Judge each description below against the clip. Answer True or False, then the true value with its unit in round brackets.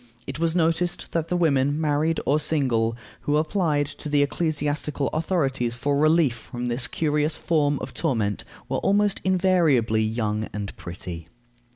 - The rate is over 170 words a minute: False (150 wpm)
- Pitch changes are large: False (4.9 semitones)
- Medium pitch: True (145 Hz)